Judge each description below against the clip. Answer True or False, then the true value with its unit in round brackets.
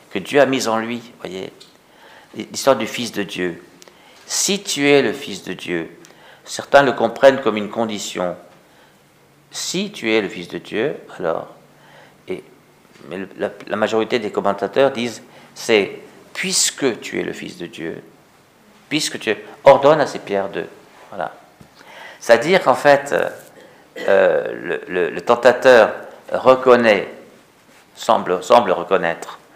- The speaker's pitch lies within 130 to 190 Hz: False (120 Hz)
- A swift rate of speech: False (145 wpm)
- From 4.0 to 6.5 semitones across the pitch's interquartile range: True (5.6 semitones)